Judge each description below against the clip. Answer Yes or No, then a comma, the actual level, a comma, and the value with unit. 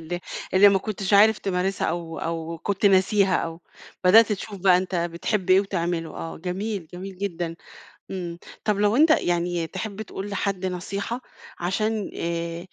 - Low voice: No, medium, 185 Hz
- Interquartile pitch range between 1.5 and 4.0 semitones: Yes, average, 2.8 semitones